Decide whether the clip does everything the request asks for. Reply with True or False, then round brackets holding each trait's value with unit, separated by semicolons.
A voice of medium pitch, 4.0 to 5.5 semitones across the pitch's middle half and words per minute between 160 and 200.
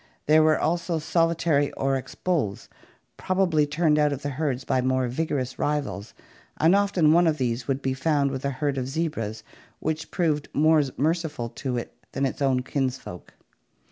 False (145 Hz; 3.4 semitones; 170 wpm)